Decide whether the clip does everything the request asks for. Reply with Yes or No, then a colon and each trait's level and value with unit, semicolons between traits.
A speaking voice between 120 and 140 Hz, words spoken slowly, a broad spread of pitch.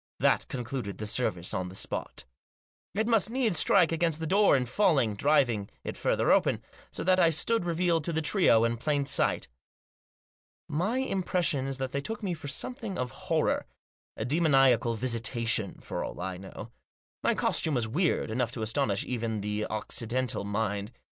No: low, 135 Hz; average, 170 wpm; wide, 7.2 semitones